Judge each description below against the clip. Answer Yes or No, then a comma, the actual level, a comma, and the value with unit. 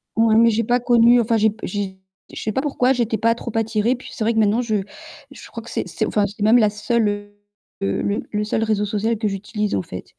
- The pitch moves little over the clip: Yes, narrow, 2.0 semitones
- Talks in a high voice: Yes, high, 220 Hz